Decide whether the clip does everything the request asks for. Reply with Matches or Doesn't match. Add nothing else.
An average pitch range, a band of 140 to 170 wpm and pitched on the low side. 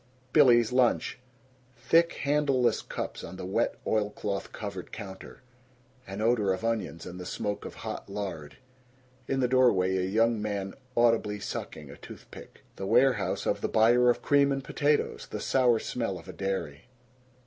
Matches